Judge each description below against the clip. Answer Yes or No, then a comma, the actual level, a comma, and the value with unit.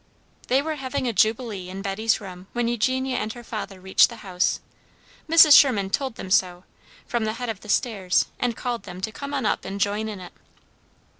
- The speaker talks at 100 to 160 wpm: No, fast, 205 wpm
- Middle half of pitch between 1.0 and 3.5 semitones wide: No, average, 4.3 semitones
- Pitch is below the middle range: No, high, 220 Hz